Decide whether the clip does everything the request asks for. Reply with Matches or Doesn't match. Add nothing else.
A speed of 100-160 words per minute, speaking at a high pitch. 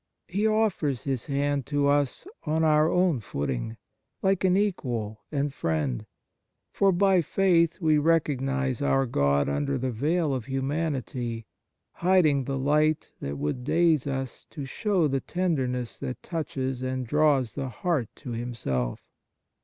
Doesn't match